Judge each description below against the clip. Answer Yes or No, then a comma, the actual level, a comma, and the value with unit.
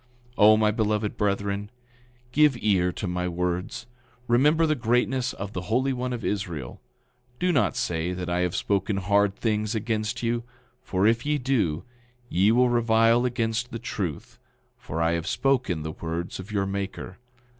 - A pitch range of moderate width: Yes, average, 4.7 semitones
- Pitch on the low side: Yes, low, 105 Hz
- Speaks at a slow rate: No, average, 165 wpm